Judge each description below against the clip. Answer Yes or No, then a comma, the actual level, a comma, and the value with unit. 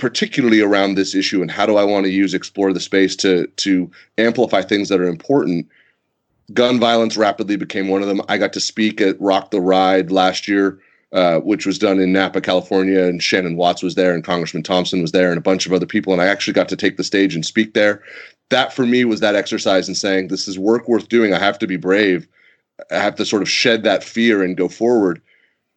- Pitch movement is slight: Yes, narrow, 2.3 semitones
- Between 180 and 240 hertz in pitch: No, very low, 95 Hz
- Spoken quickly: Yes, fast, 235 wpm